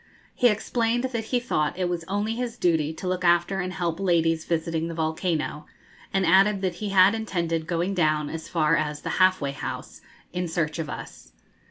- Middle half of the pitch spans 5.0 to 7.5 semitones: No, average, 3.3 semitones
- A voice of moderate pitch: Yes, medium, 175 Hz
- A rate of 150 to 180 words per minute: No, average, 195 wpm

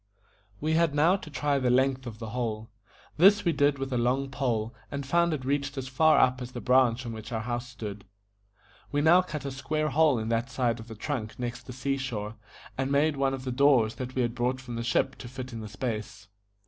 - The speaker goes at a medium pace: No, fast, 235 wpm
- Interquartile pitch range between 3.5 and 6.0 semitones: No, average, 3.0 semitones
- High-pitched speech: No, low, 130 Hz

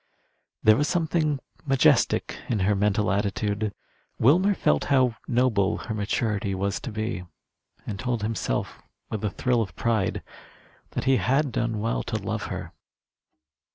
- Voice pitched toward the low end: Yes, low, 110 Hz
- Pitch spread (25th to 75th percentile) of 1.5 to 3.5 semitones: No, average, 4.0 semitones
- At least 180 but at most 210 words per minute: No, average, 145 wpm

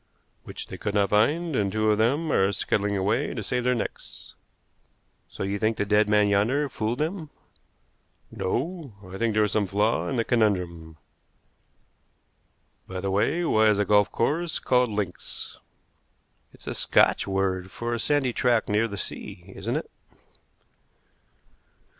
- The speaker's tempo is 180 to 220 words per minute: No, average, 160 wpm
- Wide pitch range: No, average, 3.7 semitones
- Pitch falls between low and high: No, low, 110 Hz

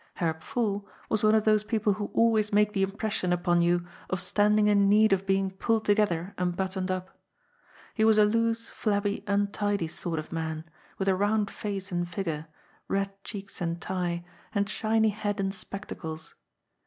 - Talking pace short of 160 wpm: No, average, 175 wpm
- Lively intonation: No, average, 2.8 semitones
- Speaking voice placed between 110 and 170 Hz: No, high, 200 Hz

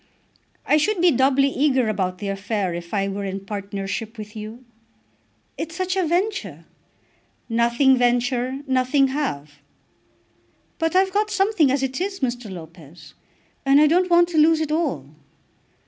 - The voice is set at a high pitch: Yes, very high, 255 Hz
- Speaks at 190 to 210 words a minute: No, average, 150 wpm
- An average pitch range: No, wide, 7.9 semitones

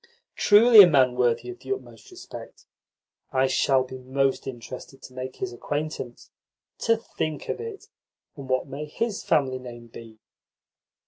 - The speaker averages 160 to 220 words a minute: No, average, 150 wpm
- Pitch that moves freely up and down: Yes, wide, 6.5 semitones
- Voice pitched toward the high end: No, low, 135 Hz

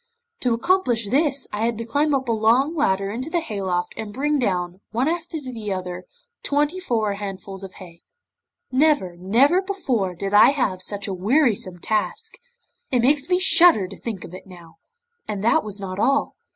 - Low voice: No, high, 225 Hz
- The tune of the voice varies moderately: No, wide, 6.8 semitones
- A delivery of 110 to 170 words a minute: No, average, 180 wpm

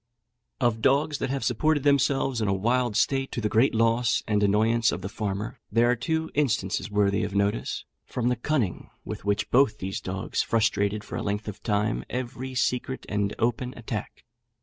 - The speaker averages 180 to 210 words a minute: Yes, average, 185 wpm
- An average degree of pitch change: Yes, average, 3.7 semitones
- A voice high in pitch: No, low, 115 Hz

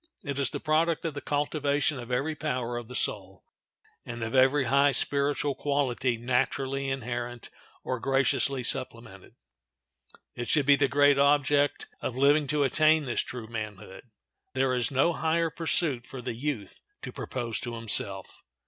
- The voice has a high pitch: No, low, 135 Hz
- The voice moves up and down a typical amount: Yes, average, 3.0 semitones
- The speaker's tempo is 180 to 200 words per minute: No, average, 155 wpm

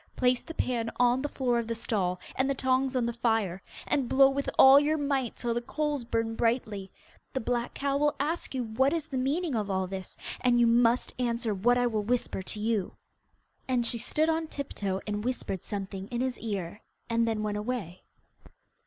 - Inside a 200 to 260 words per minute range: Yes, fast, 205 wpm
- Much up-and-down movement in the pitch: No, average, 3.6 semitones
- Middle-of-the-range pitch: No, high, 240 Hz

